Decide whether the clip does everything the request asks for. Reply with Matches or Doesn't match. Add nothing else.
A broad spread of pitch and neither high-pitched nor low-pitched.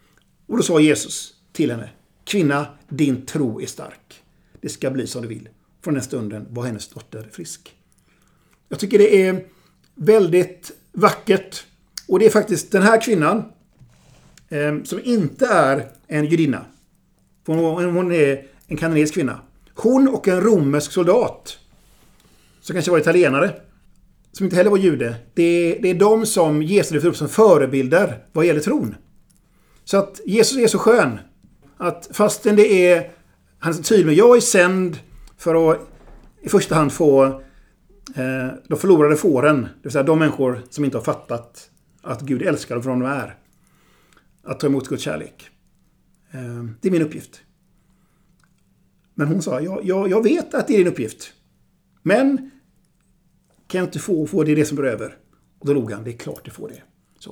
Matches